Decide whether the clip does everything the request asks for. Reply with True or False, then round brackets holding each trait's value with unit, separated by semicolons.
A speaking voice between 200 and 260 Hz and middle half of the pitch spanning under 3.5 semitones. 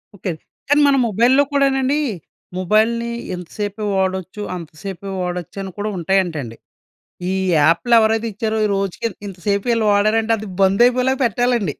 False (205 Hz; 3.8 semitones)